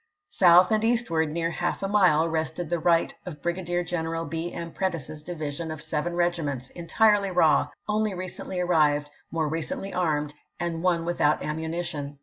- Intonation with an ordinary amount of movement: No, narrow, 2.2 semitones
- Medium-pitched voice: Yes, medium, 170 Hz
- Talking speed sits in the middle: Yes, average, 155 wpm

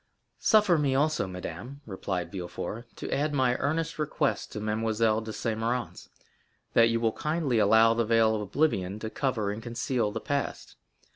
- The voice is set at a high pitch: No, low, 115 Hz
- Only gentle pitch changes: No, average, 4.5 semitones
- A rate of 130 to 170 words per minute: Yes, average, 165 wpm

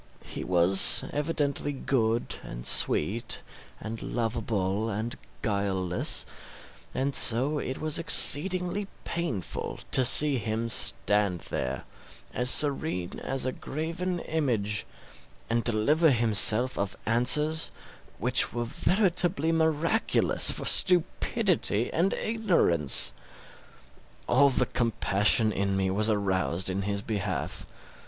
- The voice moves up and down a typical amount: No, wide, 7.1 semitones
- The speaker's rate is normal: No, slow, 105 wpm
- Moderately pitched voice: No, low, 120 Hz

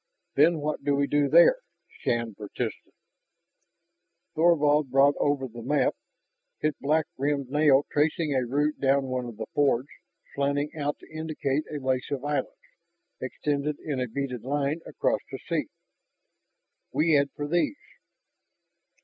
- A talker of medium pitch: Yes, medium, 145 Hz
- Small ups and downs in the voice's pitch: Yes, narrow, 2.1 semitones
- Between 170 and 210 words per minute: No, average, 140 wpm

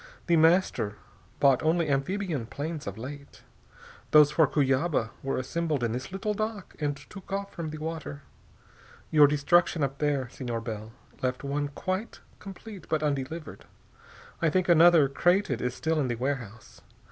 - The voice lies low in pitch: No, medium, 150 Hz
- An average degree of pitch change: Yes, average, 4.0 semitones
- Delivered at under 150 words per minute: No, average, 155 wpm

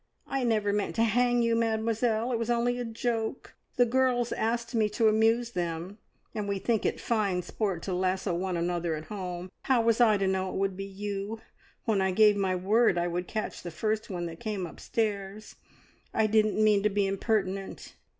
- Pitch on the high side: Yes, high, 210 Hz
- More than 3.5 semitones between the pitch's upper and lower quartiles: No, average, 3.2 semitones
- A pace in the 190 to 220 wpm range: Yes, average, 200 wpm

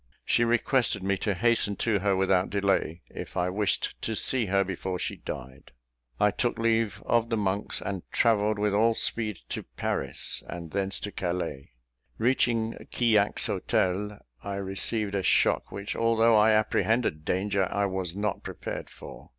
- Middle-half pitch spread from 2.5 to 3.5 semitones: Yes, average, 2.9 semitones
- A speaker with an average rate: Yes, average, 160 wpm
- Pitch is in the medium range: No, low, 100 Hz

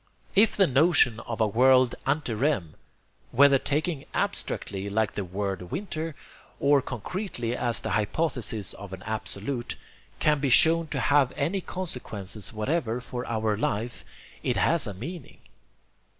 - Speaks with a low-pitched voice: Yes, low, 125 Hz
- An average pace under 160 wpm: Yes, average, 140 wpm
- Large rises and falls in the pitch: Yes, wide, 6.1 semitones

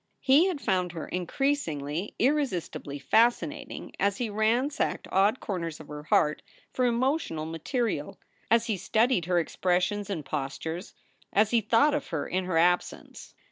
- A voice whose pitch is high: Yes, high, 195 Hz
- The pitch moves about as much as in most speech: No, wide, 6.5 semitones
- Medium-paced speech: Yes, average, 145 wpm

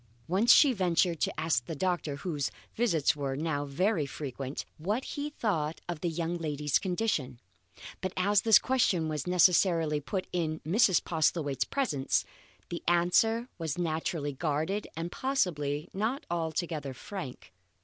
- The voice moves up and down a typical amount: Yes, average, 4.3 semitones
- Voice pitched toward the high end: No, medium, 165 Hz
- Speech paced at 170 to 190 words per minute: No, average, 140 wpm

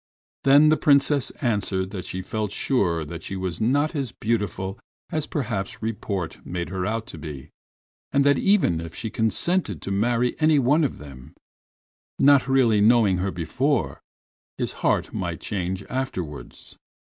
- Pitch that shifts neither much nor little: No, wide, 6.7 semitones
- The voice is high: No, low, 110 Hz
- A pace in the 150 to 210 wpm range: Yes, average, 155 wpm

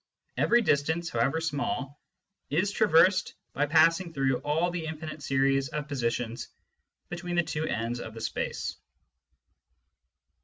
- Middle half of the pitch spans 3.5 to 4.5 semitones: Yes, average, 3.9 semitones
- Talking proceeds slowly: Yes, slow, 125 wpm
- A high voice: No, medium, 150 Hz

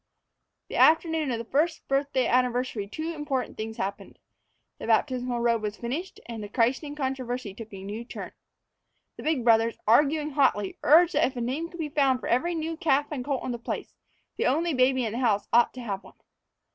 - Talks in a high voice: Yes, very high, 255 Hz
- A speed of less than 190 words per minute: No, average, 200 wpm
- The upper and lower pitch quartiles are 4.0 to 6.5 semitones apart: Yes, average, 4.3 semitones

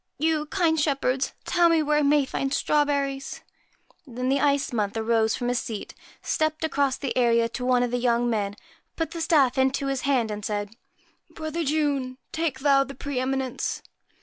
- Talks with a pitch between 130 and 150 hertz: No, very high, 270 Hz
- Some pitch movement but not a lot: Yes, average, 3.3 semitones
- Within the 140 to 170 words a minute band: No, average, 190 wpm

